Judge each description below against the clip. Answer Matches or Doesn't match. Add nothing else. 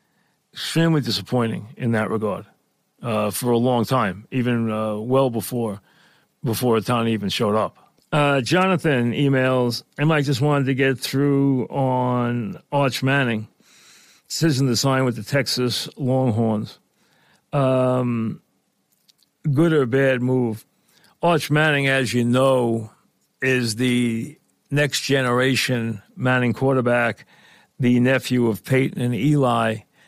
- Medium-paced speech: Doesn't match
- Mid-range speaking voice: Doesn't match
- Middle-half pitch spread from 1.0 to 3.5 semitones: Matches